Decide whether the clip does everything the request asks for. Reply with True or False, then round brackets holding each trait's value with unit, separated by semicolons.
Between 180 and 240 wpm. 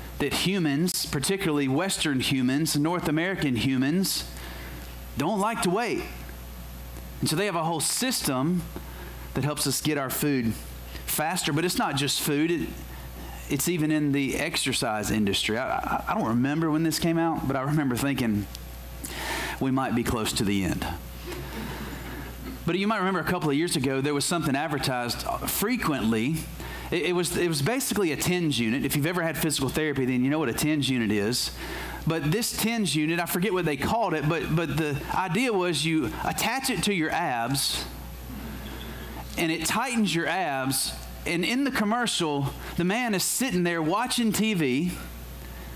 False (170 wpm)